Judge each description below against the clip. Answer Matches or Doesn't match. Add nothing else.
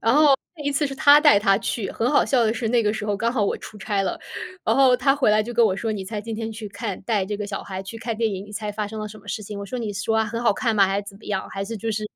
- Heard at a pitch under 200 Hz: Doesn't match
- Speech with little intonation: Matches